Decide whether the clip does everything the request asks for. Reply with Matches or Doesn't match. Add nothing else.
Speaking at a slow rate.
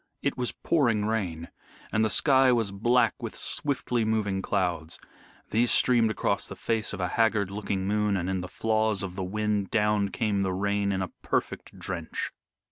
Doesn't match